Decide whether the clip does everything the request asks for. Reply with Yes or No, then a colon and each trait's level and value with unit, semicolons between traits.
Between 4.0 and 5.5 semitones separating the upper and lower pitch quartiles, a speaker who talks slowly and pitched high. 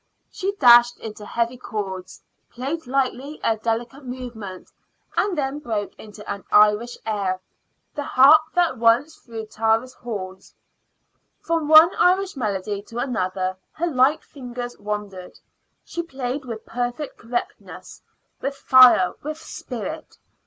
Yes: average, 4.7 semitones; slow, 125 wpm; high, 245 Hz